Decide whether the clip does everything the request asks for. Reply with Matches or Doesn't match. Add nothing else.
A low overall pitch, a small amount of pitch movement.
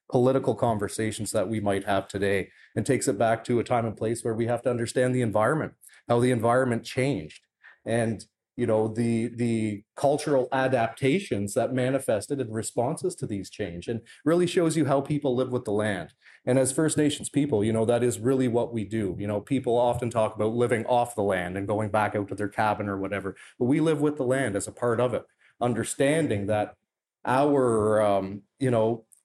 Doesn't match